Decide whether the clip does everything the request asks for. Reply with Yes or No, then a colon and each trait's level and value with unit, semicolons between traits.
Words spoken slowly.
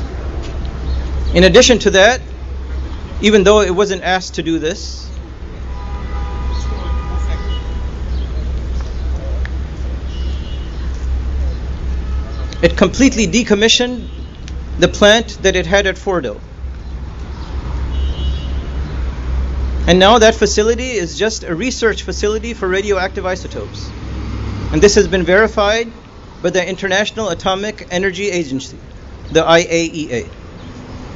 Yes: slow, 90 wpm